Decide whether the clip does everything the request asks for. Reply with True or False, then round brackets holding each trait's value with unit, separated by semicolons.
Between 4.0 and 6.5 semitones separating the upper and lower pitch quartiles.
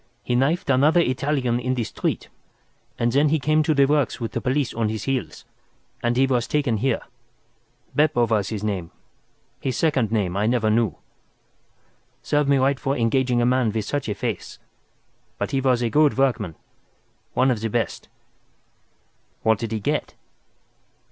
False (3.6 semitones)